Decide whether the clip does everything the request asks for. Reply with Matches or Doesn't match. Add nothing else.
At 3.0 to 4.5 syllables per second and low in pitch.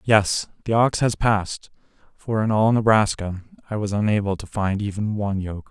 Doesn't match